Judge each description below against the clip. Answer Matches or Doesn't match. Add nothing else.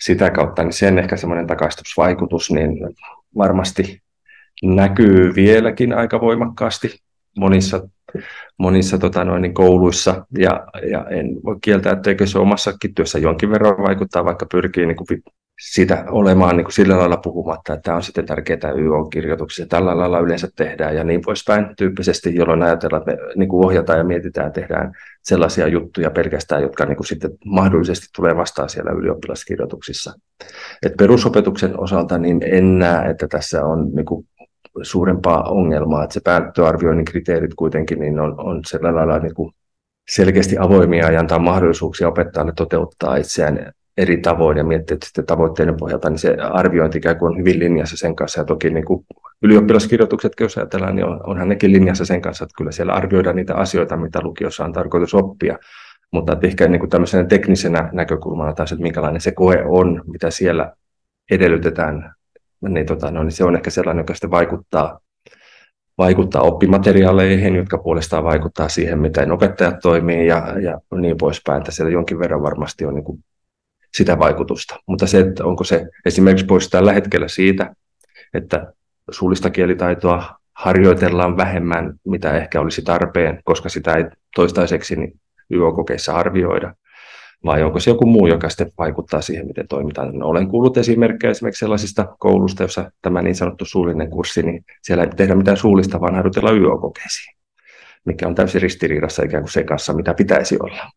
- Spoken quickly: Matches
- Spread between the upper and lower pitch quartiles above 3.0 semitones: Doesn't match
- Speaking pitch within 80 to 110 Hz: Matches